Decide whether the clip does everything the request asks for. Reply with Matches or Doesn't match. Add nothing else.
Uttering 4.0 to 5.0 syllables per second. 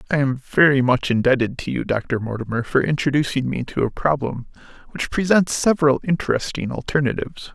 Doesn't match